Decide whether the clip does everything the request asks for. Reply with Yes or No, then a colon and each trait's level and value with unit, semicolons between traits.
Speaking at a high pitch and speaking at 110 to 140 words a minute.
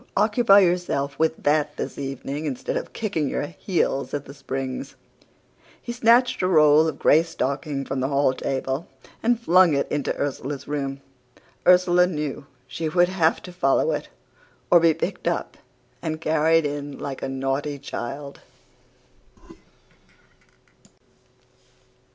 No: medium, 150 Hz; slow, 135 wpm